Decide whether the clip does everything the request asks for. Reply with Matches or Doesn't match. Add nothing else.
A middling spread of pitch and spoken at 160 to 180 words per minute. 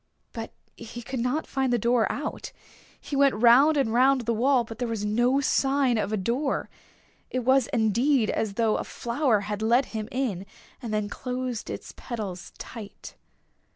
Matches